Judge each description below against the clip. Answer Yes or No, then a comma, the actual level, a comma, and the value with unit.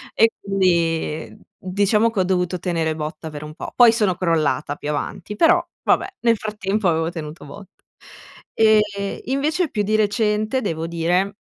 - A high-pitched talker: Yes, high, 195 Hz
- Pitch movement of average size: Yes, average, 4.7 semitones